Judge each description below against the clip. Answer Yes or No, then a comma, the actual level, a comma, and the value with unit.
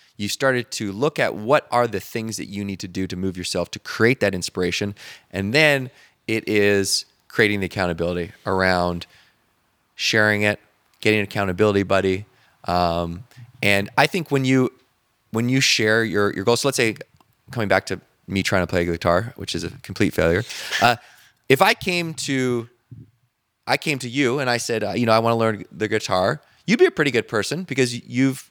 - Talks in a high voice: No, low, 110 Hz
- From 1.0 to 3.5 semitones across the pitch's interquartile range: No, average, 4.2 semitones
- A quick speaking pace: No, average, 195 wpm